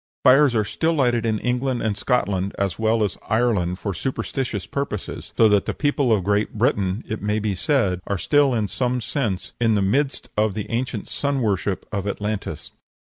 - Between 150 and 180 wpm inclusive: No, average, 190 wpm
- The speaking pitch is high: No, low, 110 Hz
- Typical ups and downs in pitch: Yes, average, 3.8 semitones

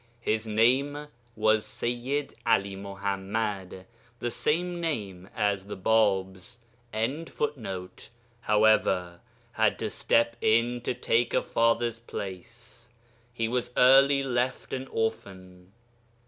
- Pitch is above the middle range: No, low, 115 Hz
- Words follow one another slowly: Yes, slow, 105 wpm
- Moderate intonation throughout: Yes, average, 3.6 semitones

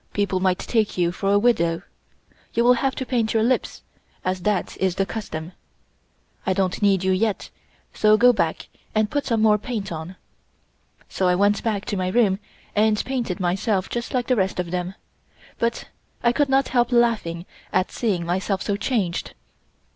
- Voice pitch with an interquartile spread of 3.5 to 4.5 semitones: Yes, average, 4.1 semitones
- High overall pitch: Yes, high, 205 Hz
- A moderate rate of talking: Yes, average, 180 wpm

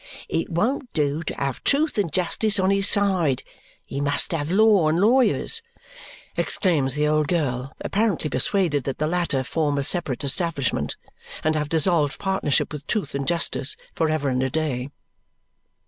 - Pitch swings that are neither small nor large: Yes, average, 4.9 semitones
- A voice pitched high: No, medium, 155 Hz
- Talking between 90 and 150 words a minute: No, average, 160 wpm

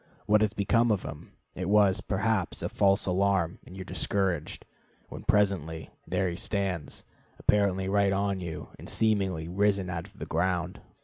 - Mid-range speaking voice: No, very low, 95 Hz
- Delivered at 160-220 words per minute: Yes, average, 170 wpm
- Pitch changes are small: Yes, narrow, 2.1 semitones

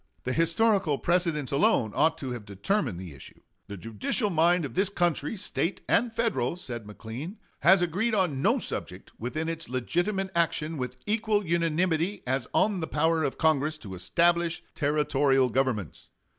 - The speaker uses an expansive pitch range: Yes, wide, 5.7 semitones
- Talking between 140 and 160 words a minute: Yes, average, 155 wpm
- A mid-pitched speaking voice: Yes, medium, 160 Hz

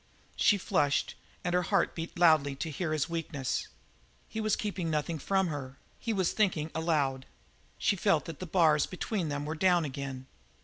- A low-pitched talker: No, medium, 160 Hz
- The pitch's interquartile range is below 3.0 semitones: No, average, 3.9 semitones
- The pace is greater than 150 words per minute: Yes, average, 175 wpm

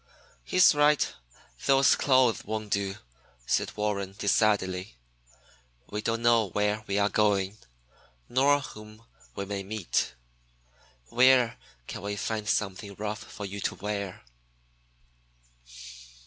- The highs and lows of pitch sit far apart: No, narrow, 2.5 semitones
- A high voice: No, low, 105 Hz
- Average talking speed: No, slow, 115 wpm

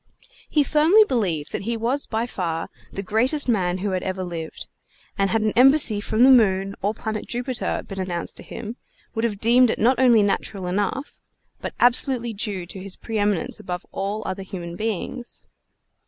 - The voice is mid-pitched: No, high, 215 Hz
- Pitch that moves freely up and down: No, average, 4.2 semitones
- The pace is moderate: Yes, average, 185 wpm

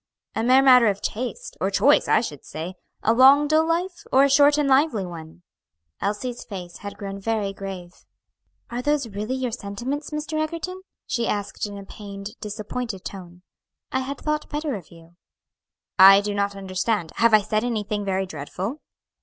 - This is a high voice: Yes, high, 215 Hz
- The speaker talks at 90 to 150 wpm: No, average, 175 wpm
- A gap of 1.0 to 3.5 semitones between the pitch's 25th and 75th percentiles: No, wide, 5.4 semitones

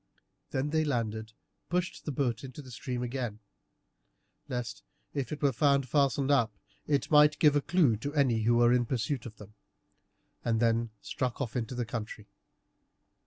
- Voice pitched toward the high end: No, low, 125 Hz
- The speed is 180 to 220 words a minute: No, average, 165 wpm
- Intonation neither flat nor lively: Yes, average, 3.7 semitones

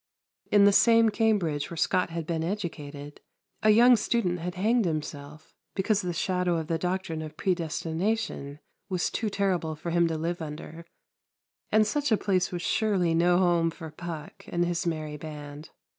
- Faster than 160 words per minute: Yes, average, 170 wpm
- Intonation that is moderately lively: Yes, average, 3.8 semitones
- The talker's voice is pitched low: No, medium, 175 Hz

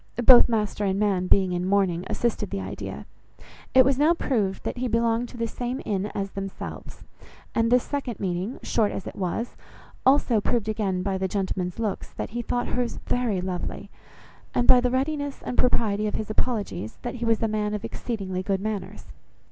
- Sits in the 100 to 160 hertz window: No, high, 215 Hz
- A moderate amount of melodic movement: Yes, average, 4.1 semitones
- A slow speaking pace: No, average, 190 wpm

